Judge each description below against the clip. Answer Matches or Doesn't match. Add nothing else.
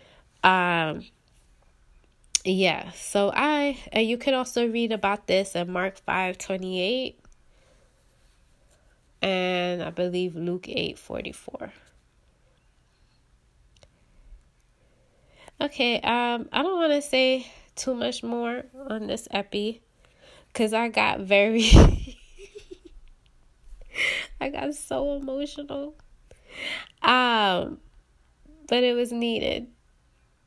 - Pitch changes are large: Matches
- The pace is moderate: Doesn't match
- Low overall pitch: Doesn't match